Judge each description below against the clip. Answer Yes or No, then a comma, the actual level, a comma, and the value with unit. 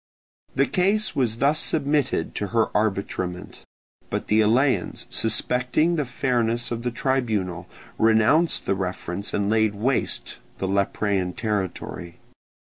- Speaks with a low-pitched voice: Yes, low, 110 Hz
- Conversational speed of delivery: No, slow, 125 wpm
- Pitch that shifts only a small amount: No, average, 4.8 semitones